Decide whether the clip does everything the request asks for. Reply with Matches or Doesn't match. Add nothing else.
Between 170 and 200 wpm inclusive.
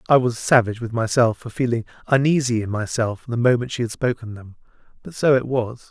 Matches